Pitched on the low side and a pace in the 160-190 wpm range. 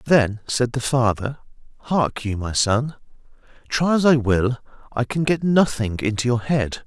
Yes: low, 125 Hz; average, 165 wpm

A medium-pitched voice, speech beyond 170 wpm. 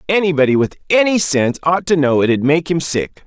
Yes: medium, 160 Hz; average, 200 wpm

